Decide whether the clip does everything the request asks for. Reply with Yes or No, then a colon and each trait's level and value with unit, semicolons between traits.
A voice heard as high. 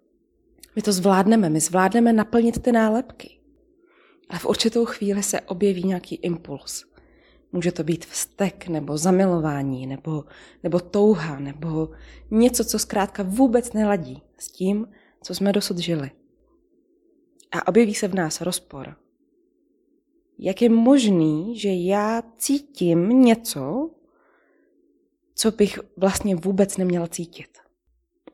Yes: high, 205 Hz